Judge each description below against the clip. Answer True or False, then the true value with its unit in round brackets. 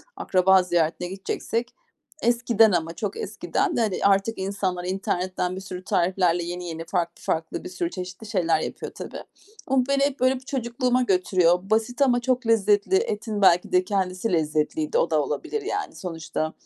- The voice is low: False (195 Hz)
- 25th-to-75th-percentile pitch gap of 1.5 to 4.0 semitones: False (5.3 semitones)